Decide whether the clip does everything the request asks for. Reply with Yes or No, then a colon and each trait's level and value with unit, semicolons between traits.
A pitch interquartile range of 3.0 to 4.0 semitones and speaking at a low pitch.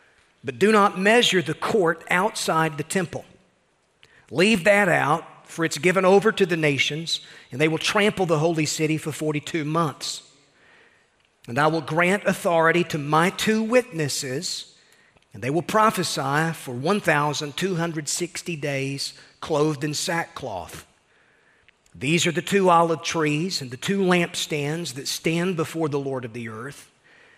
No: average, 3.6 semitones; medium, 165 Hz